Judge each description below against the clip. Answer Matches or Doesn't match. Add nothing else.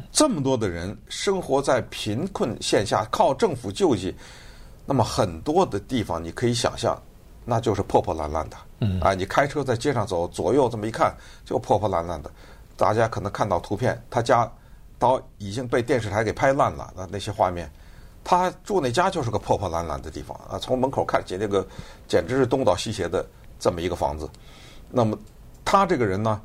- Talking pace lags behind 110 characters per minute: Doesn't match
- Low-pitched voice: Matches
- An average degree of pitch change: Doesn't match